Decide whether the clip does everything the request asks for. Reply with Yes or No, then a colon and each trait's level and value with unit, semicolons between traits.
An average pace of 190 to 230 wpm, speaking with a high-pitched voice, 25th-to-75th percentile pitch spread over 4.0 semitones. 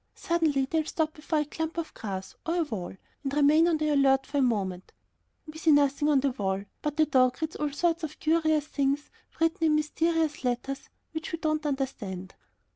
No: average, 200 wpm; very high, 300 Hz; average, 2.9 semitones